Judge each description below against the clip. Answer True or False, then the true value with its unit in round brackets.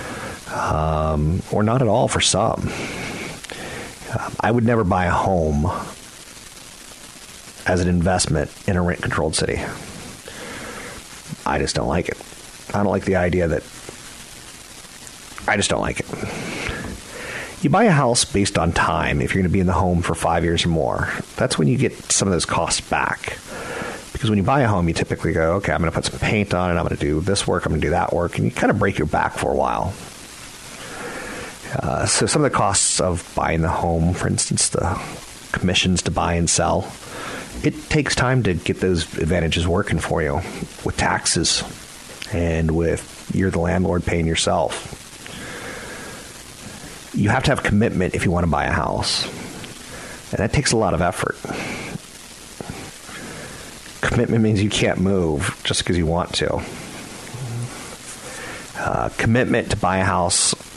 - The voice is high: False (90 Hz)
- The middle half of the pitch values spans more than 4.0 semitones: False (3.5 semitones)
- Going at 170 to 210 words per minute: True (175 wpm)